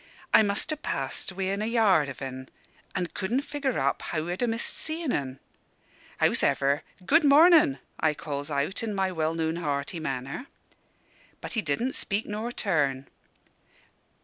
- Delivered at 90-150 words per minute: No, average, 160 wpm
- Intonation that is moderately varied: No, wide, 8.3 semitones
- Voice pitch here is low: No, medium, 185 Hz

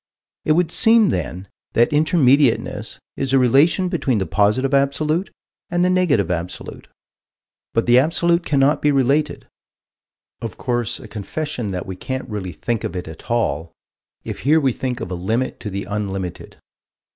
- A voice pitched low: Yes, low, 130 Hz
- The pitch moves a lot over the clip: Yes, wide, 7.0 semitones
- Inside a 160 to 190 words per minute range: Yes, average, 165 wpm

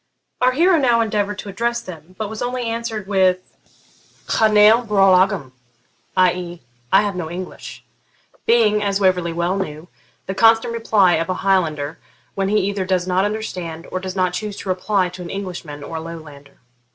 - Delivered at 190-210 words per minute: No, average, 175 wpm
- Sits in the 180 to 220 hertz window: Yes, high, 190 Hz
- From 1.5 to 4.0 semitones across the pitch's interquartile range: Yes, average, 3.1 semitones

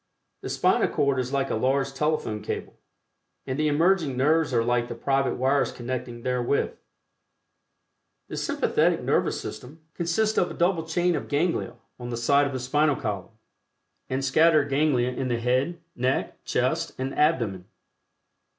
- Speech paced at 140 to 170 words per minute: Yes, average, 155 wpm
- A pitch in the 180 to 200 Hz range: No, low, 135 Hz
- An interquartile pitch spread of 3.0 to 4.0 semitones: Yes, average, 3.7 semitones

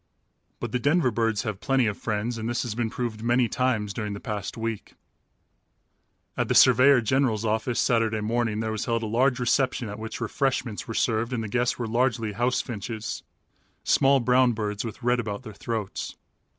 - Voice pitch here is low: Yes, low, 115 Hz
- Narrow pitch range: Yes, narrow, 2.3 semitones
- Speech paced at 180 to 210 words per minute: Yes, average, 190 wpm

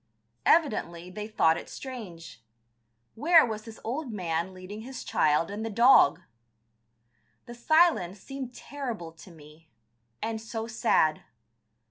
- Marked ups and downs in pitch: Yes, wide, 6.4 semitones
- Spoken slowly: Yes, slow, 125 wpm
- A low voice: No, high, 215 Hz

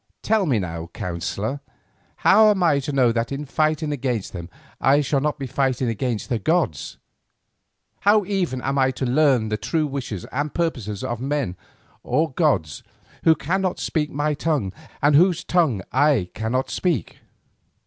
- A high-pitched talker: No, medium, 140 Hz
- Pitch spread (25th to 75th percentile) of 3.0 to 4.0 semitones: No, average, 5.1 semitones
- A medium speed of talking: Yes, average, 160 wpm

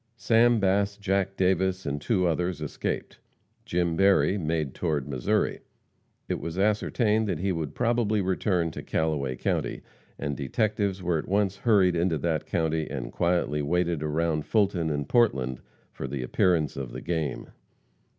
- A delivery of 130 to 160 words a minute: Yes, average, 150 wpm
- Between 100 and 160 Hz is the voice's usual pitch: No, very low, 85 Hz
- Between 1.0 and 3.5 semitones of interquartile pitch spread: No, average, 4.4 semitones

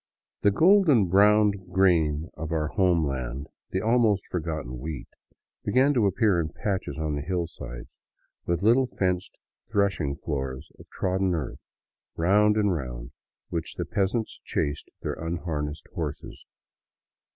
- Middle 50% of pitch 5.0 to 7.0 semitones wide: Yes, wide, 5.4 semitones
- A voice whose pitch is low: Yes, very low, 85 Hz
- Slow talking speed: Yes, slow, 130 wpm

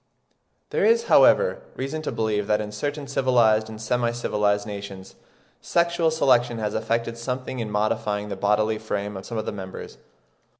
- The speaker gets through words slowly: No, average, 165 wpm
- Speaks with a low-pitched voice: Yes, low, 110 Hz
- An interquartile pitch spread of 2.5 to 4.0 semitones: Yes, average, 3.5 semitones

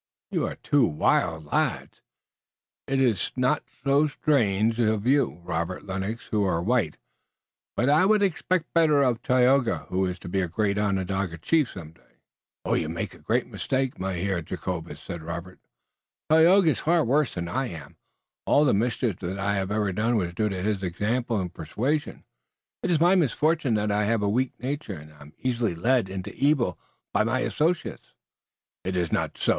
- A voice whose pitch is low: Yes, low, 110 Hz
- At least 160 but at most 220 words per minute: Yes, average, 180 wpm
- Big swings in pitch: Yes, wide, 6.5 semitones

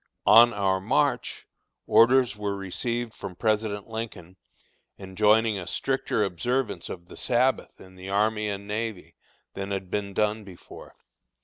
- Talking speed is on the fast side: No, slow, 135 wpm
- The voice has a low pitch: Yes, low, 105 Hz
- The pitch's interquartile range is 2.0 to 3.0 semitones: Yes, average, 2.7 semitones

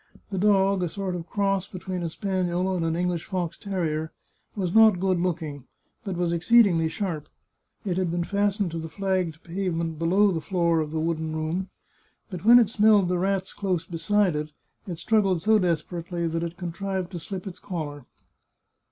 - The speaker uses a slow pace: No, average, 180 wpm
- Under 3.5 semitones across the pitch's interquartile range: Yes, average, 2.8 semitones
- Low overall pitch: No, medium, 180 Hz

